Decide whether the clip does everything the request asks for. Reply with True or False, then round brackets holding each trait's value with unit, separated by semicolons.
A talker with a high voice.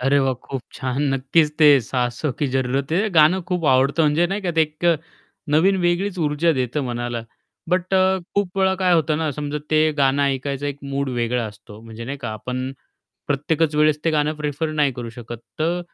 False (145 Hz)